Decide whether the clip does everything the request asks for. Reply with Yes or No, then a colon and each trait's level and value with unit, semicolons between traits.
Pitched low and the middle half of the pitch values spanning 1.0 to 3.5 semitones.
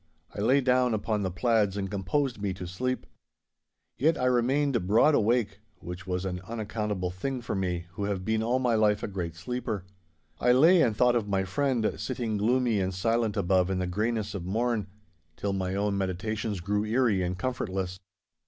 No: low, 105 Hz; average, 4.3 semitones